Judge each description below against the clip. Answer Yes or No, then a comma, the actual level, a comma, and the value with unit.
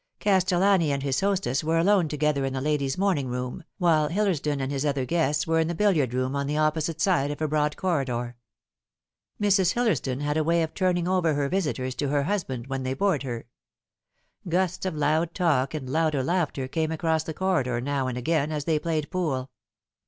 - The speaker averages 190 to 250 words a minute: Yes, average, 200 wpm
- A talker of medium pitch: Yes, medium, 155 Hz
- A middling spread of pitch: Yes, average, 4.1 semitones